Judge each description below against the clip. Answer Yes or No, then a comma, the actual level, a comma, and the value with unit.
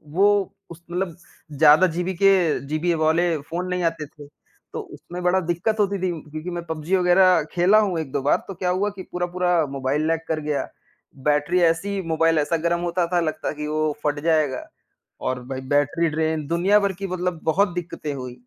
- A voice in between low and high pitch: Yes, medium, 170 Hz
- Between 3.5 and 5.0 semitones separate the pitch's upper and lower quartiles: No, average, 2.8 semitones